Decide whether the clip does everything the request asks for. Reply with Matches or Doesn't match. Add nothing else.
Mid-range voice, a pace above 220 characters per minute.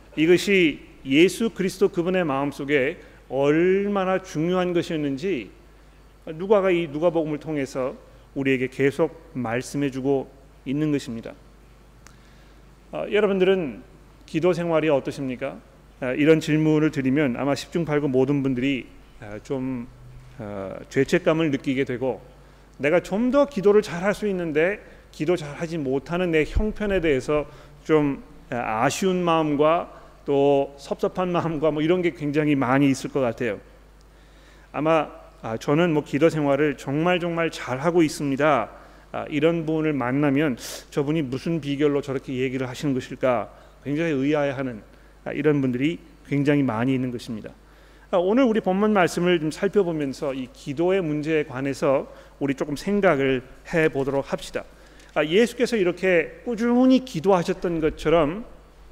Matches